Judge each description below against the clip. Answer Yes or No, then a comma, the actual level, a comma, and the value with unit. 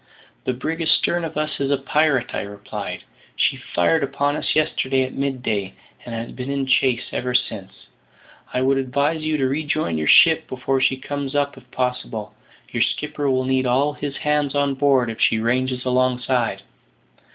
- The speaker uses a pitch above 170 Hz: No, low, 130 Hz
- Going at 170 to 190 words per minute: Yes, average, 180 wpm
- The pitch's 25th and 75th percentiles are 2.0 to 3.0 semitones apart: Yes, narrow, 2.4 semitones